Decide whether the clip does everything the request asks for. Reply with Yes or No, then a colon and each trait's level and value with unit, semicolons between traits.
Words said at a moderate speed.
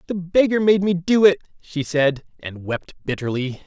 Yes: average, 180 wpm